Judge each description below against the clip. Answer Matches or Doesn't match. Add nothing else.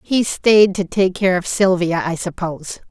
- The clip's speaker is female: Matches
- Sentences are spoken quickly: Doesn't match